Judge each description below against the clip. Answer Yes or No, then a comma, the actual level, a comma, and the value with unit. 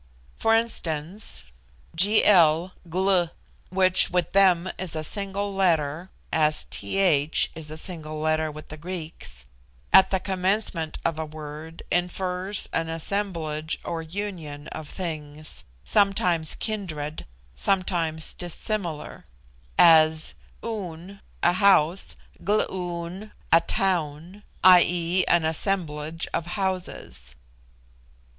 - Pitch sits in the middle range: Yes, medium, 170 Hz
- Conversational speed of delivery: No, slow, 105 wpm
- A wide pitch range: No, average, 3.4 semitones